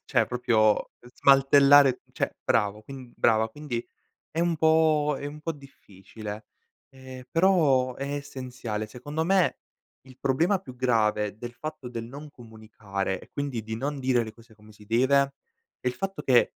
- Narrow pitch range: No, average, 4.4 semitones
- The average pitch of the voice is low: Yes, low, 130 Hz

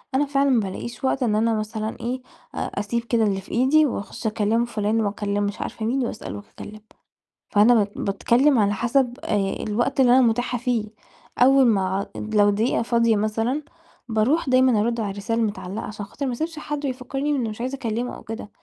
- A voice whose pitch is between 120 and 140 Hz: No, high, 230 Hz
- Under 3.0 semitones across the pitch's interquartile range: No, average, 3.3 semitones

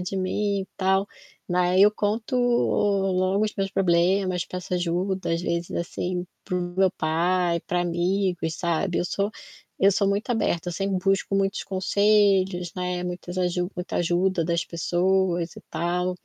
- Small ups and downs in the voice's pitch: Yes, narrow, 1.7 semitones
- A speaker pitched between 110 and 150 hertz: No, medium, 185 Hz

